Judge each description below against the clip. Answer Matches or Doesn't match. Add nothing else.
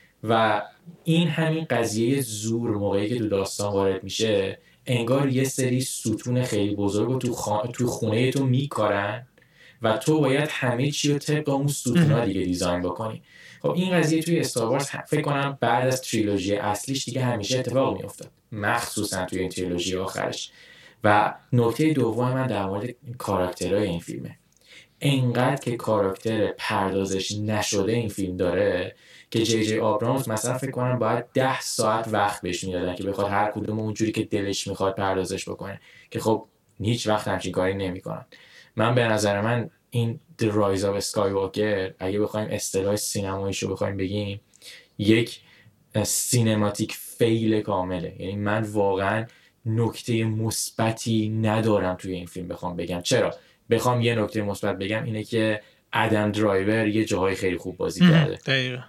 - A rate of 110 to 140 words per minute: Doesn't match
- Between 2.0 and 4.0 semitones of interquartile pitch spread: Matches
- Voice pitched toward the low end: Matches